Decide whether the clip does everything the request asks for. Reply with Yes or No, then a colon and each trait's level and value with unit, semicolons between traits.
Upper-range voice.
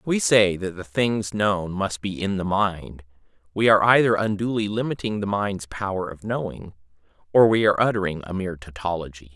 No: low, 100 Hz